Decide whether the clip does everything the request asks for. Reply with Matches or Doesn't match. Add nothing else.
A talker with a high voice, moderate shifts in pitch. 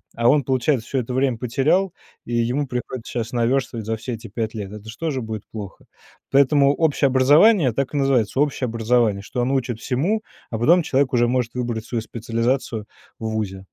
Doesn't match